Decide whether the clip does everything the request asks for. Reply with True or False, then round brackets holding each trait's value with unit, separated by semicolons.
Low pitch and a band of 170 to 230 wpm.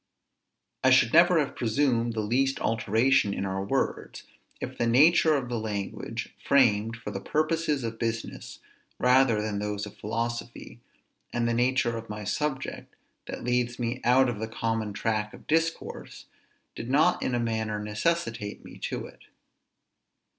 False (115 Hz; 155 wpm)